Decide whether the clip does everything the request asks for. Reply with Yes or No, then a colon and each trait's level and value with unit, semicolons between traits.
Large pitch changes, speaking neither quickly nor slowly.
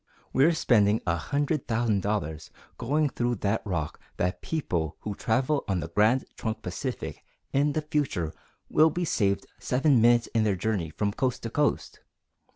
Yes: wide, 6.0 semitones; average, 160 wpm